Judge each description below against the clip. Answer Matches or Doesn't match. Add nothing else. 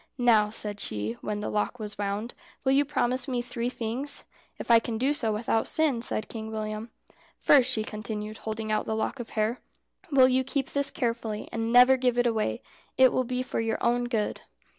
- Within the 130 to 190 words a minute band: Doesn't match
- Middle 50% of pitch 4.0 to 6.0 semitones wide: Doesn't match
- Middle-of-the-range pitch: Doesn't match